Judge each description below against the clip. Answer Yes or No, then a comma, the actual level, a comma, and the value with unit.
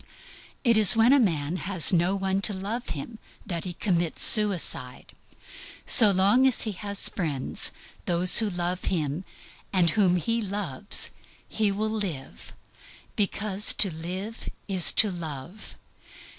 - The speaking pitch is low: No, high, 190 Hz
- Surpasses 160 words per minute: No, average, 140 wpm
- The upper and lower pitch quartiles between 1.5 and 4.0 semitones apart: Yes, average, 3.6 semitones